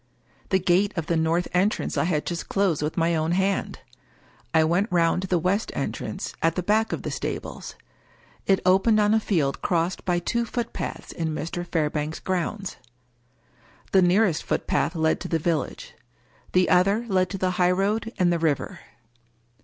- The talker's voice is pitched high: No, medium, 180 Hz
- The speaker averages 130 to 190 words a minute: Yes, average, 175 wpm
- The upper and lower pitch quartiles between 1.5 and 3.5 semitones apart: Yes, average, 3.0 semitones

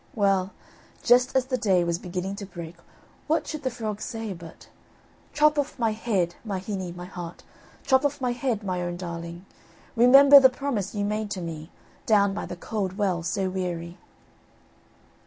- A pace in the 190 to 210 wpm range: No, average, 175 wpm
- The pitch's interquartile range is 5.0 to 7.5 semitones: Yes, average, 5.3 semitones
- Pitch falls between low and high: No, high, 200 Hz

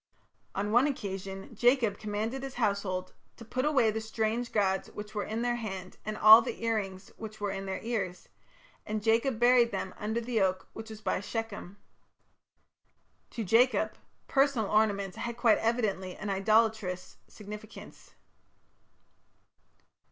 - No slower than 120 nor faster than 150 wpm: Yes, average, 145 wpm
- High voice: Yes, high, 215 Hz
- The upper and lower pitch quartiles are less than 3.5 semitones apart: Yes, average, 2.7 semitones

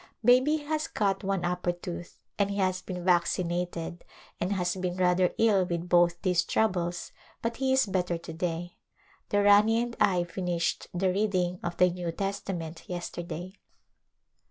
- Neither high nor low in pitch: Yes, medium, 180 Hz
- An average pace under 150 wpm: No, average, 160 wpm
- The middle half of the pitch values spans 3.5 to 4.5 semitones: No, narrow, 2.4 semitones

